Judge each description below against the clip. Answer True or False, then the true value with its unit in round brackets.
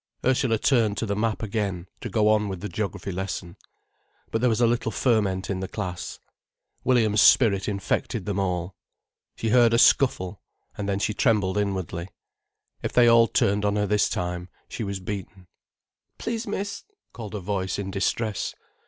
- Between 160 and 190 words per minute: True (170 wpm)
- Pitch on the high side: False (105 Hz)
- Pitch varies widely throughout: False (3.0 semitones)